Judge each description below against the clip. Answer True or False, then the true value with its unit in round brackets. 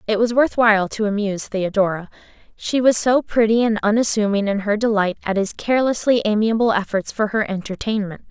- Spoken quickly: False (175 wpm)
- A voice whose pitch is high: True (215 Hz)